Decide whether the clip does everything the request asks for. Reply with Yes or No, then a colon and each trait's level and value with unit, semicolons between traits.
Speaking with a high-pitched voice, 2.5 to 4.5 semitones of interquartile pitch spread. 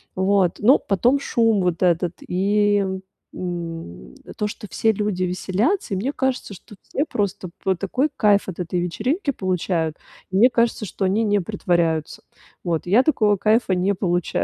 Yes: high, 195 Hz; average, 3.5 semitones